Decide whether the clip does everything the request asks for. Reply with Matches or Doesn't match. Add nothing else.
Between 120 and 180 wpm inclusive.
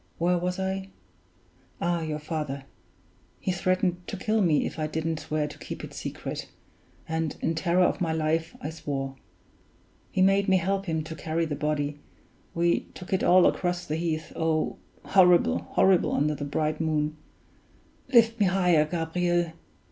Matches